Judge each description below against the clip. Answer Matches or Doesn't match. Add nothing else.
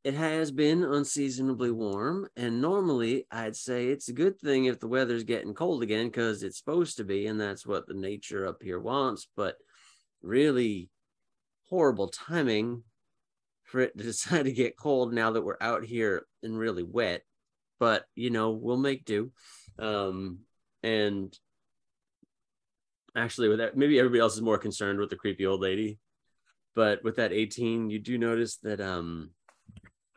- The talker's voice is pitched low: Matches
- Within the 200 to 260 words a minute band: Doesn't match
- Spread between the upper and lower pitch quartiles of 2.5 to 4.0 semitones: Matches